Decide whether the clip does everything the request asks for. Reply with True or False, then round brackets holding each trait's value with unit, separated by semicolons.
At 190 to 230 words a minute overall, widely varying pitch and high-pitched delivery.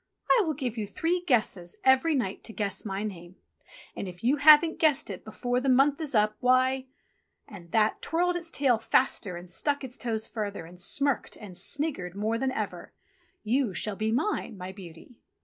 True (200 wpm; 5.8 semitones; 230 Hz)